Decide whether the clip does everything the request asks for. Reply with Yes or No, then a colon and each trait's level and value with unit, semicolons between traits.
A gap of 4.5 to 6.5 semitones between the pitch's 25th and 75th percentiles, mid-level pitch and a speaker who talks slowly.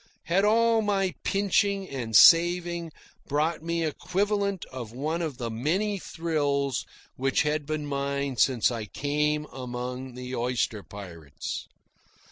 Yes: wide, 5.6 semitones; medium, 150 Hz; slow, 130 wpm